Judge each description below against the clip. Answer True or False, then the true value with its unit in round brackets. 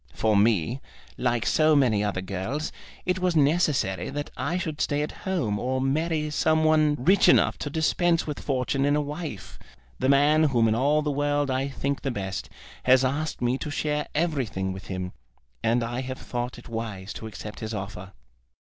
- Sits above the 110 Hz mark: True (135 Hz)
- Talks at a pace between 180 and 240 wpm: True (185 wpm)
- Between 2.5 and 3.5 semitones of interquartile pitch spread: False (5.1 semitones)